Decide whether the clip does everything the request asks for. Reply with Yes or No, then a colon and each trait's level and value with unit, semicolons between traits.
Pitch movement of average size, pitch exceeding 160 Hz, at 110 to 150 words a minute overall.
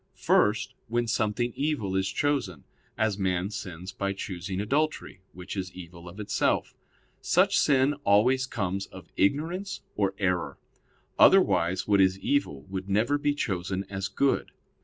No: average, 4.6 semitones; low, 100 Hz; average, 140 wpm